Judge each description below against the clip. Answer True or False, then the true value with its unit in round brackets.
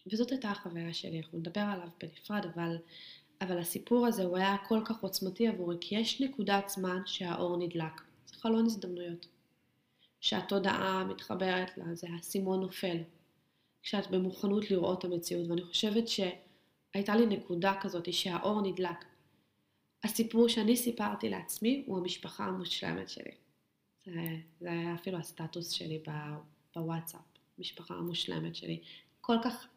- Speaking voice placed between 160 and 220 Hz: True (185 Hz)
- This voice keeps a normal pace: True (135 wpm)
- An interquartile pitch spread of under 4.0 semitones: True (3.0 semitones)